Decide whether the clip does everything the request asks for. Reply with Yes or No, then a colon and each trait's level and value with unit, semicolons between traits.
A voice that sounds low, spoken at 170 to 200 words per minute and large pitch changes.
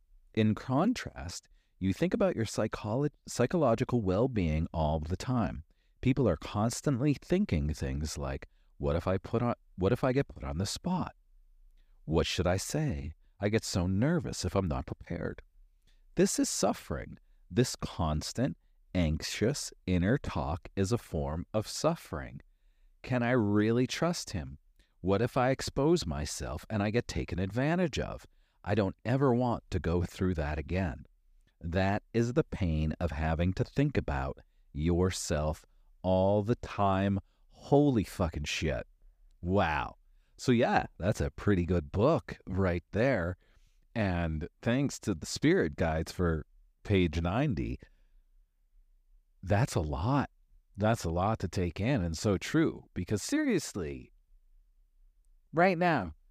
No: very low, 95 Hz; average, 140 wpm; wide, 6.6 semitones